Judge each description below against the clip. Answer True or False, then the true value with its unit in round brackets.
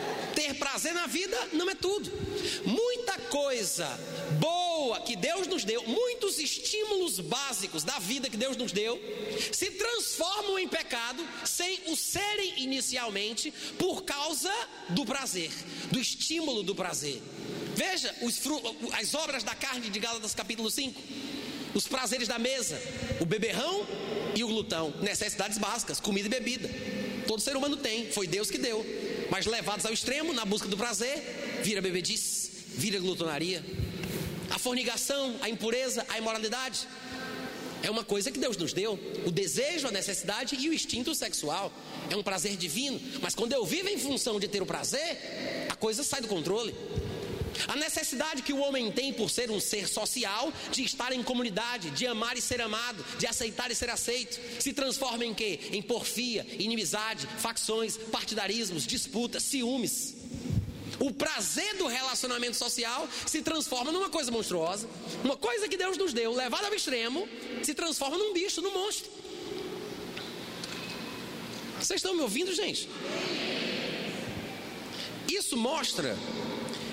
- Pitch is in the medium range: False (250 Hz)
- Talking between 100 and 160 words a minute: True (150 wpm)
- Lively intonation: True (5.8 semitones)